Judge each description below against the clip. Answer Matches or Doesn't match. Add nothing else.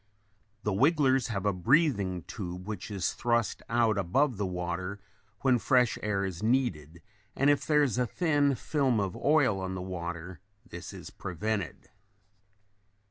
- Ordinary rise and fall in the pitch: Doesn't match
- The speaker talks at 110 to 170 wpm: Matches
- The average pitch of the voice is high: Doesn't match